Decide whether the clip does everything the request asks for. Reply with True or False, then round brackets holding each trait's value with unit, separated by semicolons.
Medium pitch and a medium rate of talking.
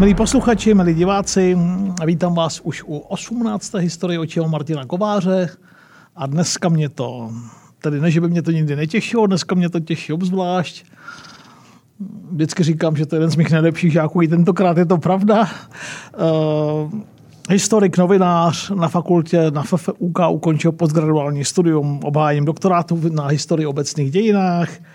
True (170 Hz; 145 wpm)